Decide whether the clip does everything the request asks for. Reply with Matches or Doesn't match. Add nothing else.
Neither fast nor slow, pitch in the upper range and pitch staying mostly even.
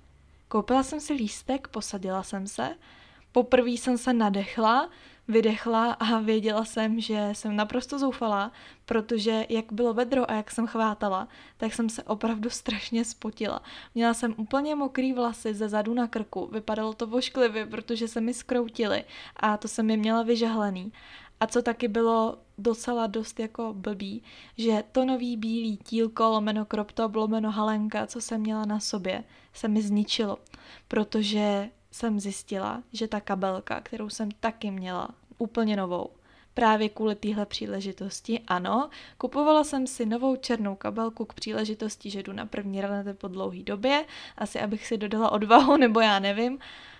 Matches